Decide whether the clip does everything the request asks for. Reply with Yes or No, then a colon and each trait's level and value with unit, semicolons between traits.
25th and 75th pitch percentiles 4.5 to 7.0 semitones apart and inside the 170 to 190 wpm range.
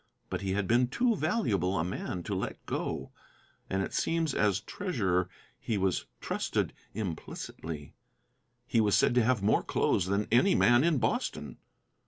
No: average, 5.2 semitones; average, 160 wpm